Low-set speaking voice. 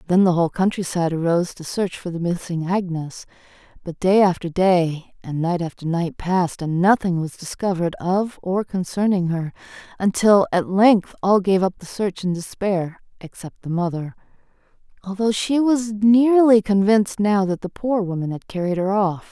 No: medium, 185 Hz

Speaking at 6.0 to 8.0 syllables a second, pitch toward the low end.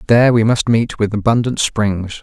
No: 4.9 syllables/s; low, 110 Hz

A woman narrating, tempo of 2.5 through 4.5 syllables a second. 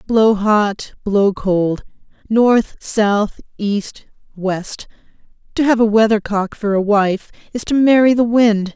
Yes: female; 3.5 syllables/s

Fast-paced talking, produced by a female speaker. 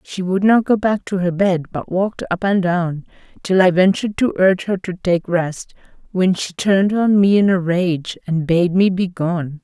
Yes: fast, 220 wpm; female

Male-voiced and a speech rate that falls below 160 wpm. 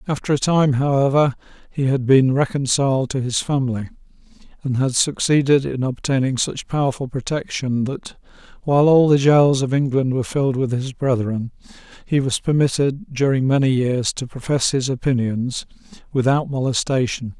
Yes: male; average, 150 wpm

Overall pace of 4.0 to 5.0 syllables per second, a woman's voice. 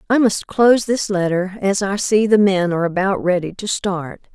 Yes: 4.9 syllables/s; female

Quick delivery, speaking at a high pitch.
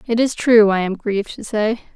Yes: fast, 245 wpm; high, 215 Hz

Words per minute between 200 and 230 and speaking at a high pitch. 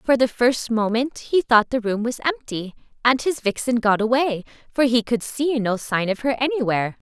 Yes: fast, 205 wpm; high, 240 Hz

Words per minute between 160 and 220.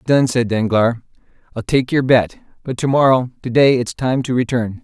Yes: average, 200 wpm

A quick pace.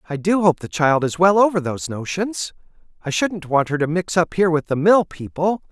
Yes: fast, 230 wpm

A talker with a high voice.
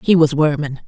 No: medium, 155 Hz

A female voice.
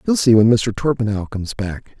No: male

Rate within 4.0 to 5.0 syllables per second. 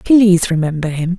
No: 5.2 syllables/s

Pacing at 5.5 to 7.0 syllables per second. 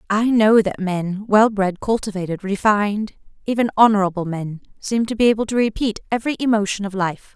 Yes: 5.6 syllables/s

